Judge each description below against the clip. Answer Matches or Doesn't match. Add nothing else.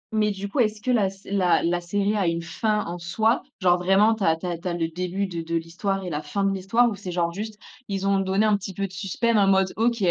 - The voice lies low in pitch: Doesn't match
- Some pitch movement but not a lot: Matches